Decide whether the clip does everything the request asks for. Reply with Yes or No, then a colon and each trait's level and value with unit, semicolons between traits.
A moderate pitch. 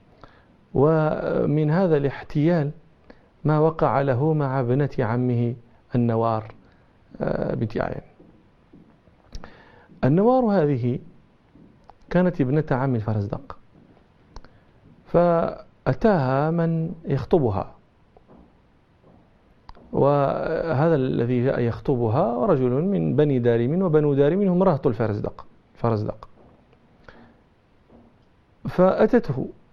Yes: medium, 145 Hz